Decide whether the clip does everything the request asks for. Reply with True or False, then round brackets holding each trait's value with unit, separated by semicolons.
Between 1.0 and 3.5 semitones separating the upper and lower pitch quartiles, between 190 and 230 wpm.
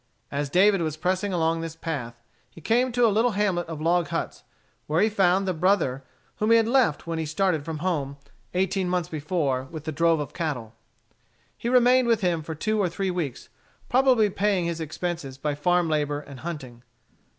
False (4.5 semitones; 195 wpm)